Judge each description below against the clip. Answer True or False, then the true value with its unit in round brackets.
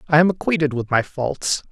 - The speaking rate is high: True (210 wpm)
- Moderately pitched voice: True (150 Hz)